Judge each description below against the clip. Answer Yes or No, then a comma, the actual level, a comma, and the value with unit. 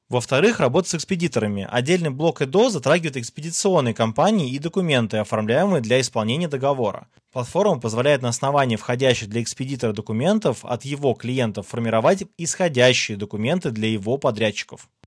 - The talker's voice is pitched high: No, low, 130 Hz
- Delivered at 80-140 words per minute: Yes, average, 130 wpm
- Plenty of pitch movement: Yes, wide, 6.3 semitones